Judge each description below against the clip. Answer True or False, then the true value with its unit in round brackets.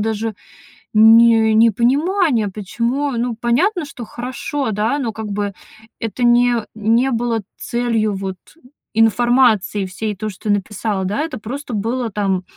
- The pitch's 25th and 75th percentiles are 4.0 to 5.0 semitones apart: False (2.7 semitones)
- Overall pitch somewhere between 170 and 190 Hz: False (225 Hz)